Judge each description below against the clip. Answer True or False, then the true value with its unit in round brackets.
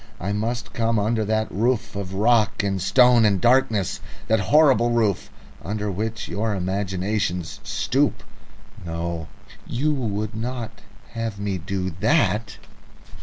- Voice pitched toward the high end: False (105 Hz)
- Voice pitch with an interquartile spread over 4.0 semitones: False (2.9 semitones)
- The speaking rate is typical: False (125 wpm)